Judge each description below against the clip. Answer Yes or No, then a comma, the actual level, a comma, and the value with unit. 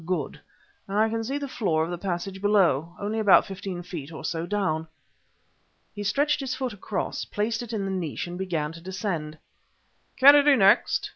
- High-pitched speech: Yes, high, 195 Hz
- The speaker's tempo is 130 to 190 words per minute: Yes, average, 180 wpm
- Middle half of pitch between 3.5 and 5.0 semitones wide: Yes, average, 4.3 semitones